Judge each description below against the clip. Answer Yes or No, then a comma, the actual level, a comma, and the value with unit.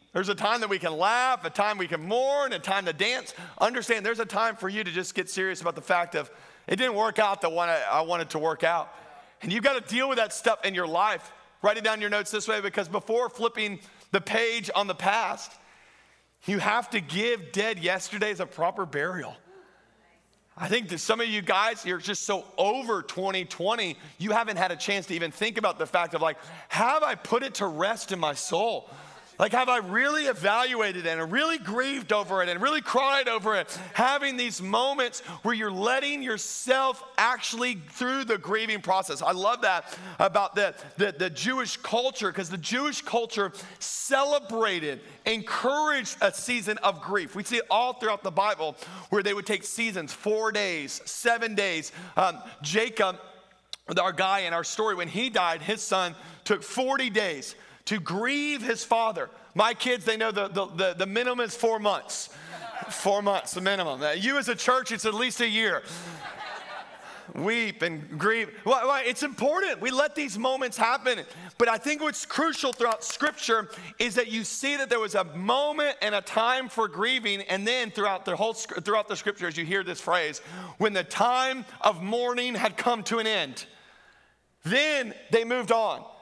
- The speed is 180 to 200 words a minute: Yes, average, 190 wpm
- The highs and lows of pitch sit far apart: No, average, 4.3 semitones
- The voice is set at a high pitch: Yes, high, 215 Hz